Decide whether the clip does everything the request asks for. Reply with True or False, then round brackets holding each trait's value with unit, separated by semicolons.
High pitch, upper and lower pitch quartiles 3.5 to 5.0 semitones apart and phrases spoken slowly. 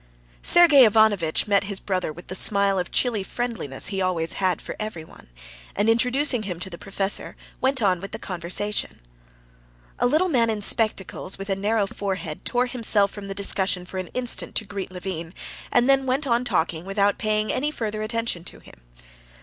False (205 Hz; 3.8 semitones; 180 wpm)